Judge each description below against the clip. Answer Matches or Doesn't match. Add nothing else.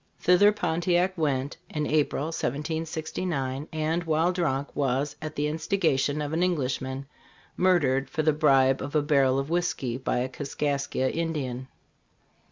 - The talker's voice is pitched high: Doesn't match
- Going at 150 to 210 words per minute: Doesn't match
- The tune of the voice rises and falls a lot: Doesn't match